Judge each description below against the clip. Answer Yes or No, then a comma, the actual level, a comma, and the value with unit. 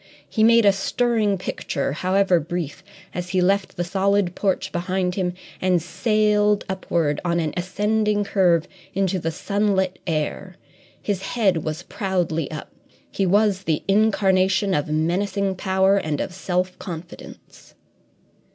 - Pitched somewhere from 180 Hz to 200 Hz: Yes, high, 190 Hz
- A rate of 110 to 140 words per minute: Yes, slow, 135 wpm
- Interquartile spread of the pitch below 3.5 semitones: Yes, narrow, 2.4 semitones